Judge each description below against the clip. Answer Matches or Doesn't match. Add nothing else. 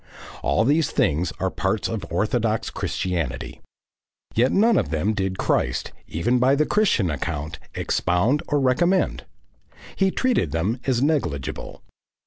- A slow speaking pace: Matches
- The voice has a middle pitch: Doesn't match